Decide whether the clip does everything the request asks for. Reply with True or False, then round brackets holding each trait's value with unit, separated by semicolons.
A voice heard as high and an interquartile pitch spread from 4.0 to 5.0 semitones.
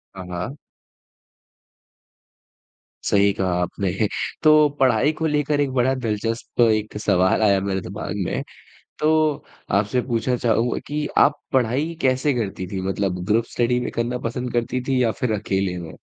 False (115 Hz; 4.6 semitones)